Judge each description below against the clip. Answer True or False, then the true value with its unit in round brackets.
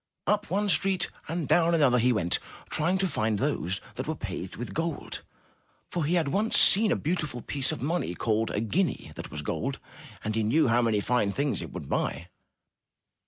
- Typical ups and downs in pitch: False (7.5 semitones)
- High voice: False (140 Hz)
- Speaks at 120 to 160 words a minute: False (195 wpm)